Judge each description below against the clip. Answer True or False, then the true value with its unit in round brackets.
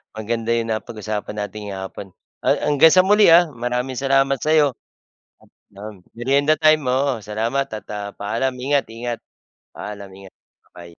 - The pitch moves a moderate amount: True (4.6 semitones)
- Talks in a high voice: False (120 Hz)